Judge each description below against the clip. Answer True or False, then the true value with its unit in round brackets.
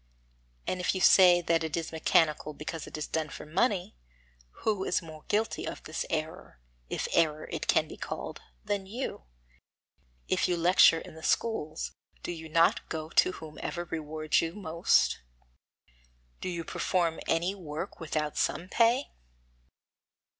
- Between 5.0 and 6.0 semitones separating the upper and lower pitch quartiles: False (2.7 semitones)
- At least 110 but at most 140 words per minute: False (155 wpm)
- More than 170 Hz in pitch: False (165 Hz)